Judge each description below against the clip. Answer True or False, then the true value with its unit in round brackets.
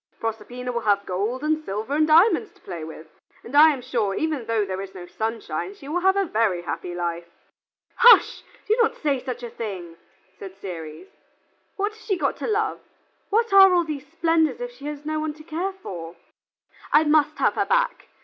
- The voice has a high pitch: True (280 Hz)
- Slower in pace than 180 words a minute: False (200 wpm)